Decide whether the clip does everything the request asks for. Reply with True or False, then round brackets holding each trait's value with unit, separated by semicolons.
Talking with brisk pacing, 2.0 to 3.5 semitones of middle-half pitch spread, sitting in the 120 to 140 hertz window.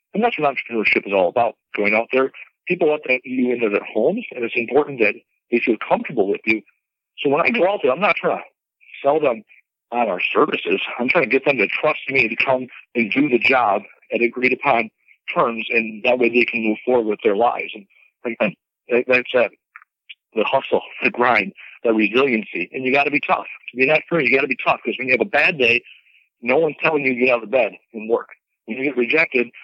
True (235 wpm; 2.9 semitones; 125 Hz)